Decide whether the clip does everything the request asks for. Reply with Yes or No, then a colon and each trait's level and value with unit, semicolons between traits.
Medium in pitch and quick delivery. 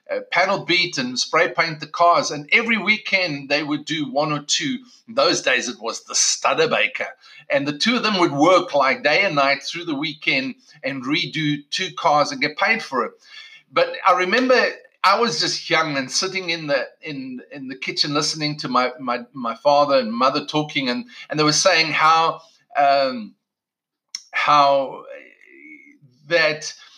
No: medium, 170 Hz; average, 180 wpm